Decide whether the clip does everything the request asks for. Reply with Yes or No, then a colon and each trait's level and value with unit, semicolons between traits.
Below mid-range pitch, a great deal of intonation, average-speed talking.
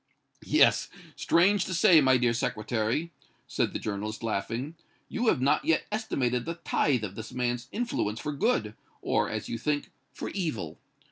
Yes: low, 125 Hz; wide, 6.8 semitones; average, 160 wpm